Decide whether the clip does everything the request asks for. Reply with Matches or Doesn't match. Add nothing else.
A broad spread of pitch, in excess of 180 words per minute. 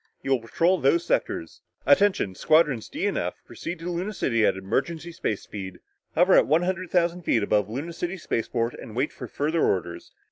Matches